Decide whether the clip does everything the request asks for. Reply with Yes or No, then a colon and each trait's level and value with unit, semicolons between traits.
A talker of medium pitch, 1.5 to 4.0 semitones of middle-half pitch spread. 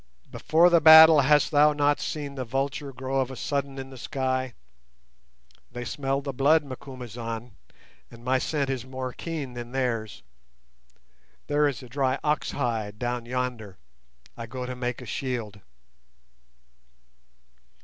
No: low, 130 Hz; narrow, 2.6 semitones